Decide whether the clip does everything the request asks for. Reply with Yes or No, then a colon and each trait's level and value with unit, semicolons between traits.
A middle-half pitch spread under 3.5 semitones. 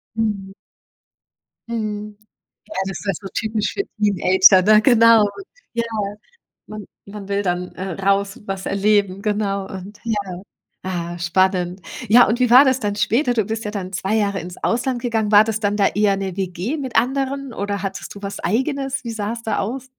Yes: average, 2.8 semitones